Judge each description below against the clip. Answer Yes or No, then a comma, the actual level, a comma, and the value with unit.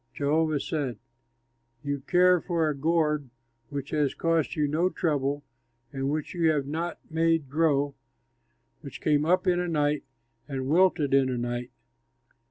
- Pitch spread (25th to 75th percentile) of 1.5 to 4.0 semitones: Yes, average, 2.8 semitones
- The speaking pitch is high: No, medium, 150 Hz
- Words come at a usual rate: Yes, average, 150 wpm